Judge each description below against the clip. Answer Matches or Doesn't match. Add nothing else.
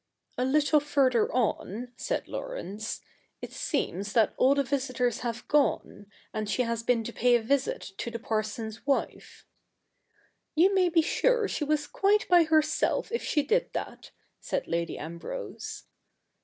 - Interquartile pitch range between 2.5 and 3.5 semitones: Doesn't match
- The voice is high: Matches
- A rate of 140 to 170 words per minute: Matches